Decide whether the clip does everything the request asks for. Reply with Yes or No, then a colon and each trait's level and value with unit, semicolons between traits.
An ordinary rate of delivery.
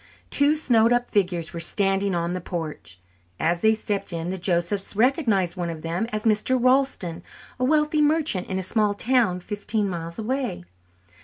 Yes: average, 170 wpm